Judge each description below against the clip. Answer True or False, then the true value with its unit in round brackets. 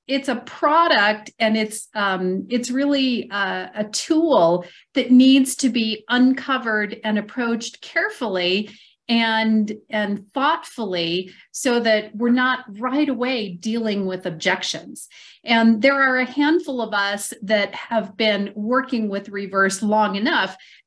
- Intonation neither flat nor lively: True (3.9 semitones)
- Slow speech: True (130 wpm)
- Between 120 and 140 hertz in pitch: False (225 Hz)